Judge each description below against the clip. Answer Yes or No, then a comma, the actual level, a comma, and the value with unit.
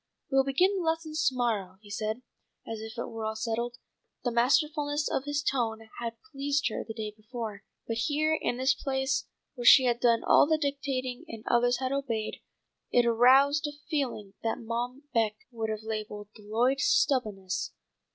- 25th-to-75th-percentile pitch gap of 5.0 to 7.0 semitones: No, average, 3.9 semitones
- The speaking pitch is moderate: No, high, 245 Hz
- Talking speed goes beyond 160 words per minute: Yes, average, 180 wpm